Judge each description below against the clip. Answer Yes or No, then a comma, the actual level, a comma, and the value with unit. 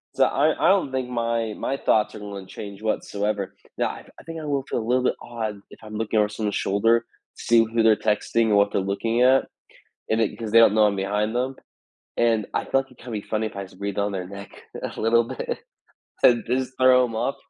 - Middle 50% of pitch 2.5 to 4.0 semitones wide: Yes, average, 2.9 semitones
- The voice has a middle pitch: No, low, 110 Hz